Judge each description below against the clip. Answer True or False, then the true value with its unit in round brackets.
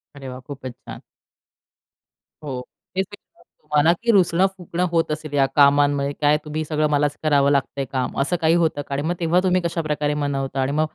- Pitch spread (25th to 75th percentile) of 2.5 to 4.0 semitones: True (2.9 semitones)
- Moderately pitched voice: True (150 Hz)